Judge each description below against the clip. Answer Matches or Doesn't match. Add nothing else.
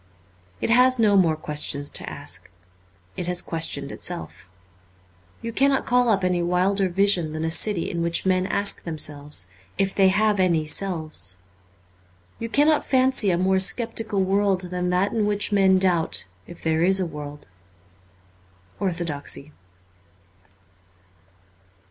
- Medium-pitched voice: Matches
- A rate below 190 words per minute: Matches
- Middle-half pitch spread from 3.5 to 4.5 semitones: Matches